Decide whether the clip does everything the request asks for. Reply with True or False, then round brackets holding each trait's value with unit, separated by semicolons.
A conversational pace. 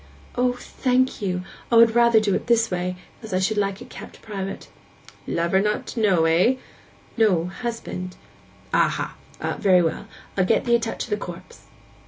True (170 wpm)